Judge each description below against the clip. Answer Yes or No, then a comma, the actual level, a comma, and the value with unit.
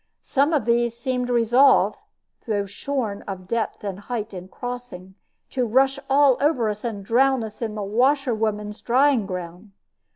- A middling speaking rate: Yes, average, 160 wpm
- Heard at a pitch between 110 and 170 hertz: No, high, 235 Hz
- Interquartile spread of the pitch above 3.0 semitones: Yes, average, 4.0 semitones